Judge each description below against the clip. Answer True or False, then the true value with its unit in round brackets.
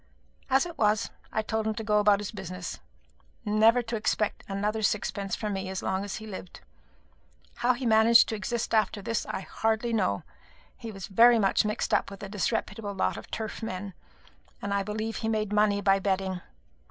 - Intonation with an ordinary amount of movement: False (2.2 semitones)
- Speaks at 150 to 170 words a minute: False (195 wpm)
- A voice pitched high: True (210 Hz)